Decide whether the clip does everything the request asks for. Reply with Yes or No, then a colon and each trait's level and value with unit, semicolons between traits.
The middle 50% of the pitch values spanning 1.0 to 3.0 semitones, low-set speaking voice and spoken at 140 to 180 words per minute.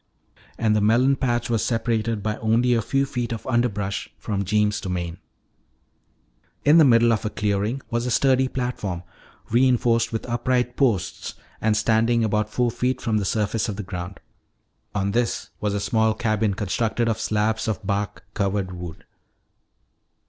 Yes: narrow, 2.6 semitones; low, 110 Hz; average, 160 wpm